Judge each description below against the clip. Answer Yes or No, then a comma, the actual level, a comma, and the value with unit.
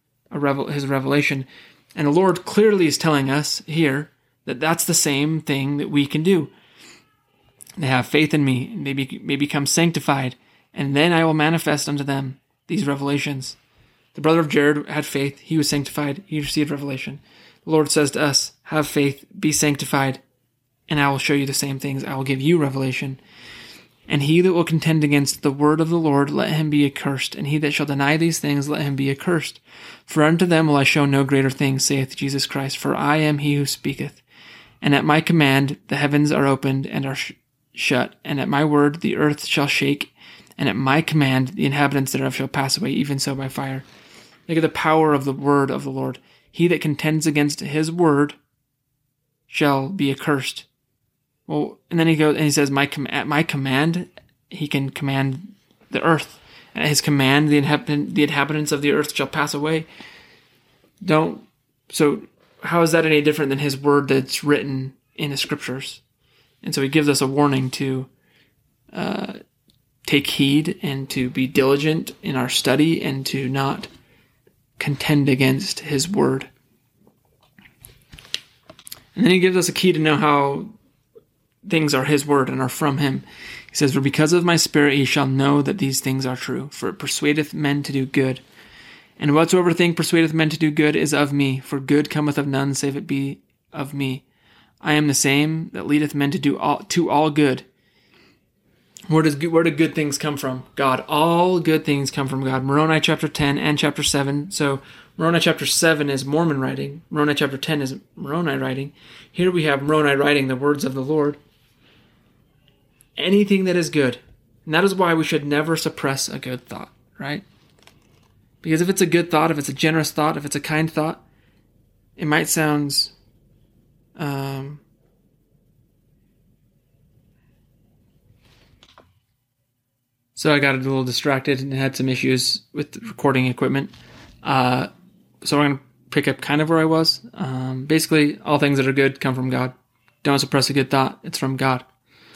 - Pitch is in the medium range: Yes, medium, 145 Hz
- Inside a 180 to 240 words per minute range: Yes, average, 185 wpm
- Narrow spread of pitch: Yes, narrow, 2.3 semitones